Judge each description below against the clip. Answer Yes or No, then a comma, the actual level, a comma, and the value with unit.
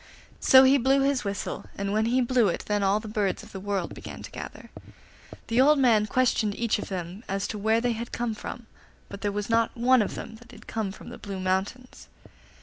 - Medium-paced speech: No, fast, 230 wpm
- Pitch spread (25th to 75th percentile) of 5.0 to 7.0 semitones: No, average, 3.3 semitones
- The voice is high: Yes, high, 220 Hz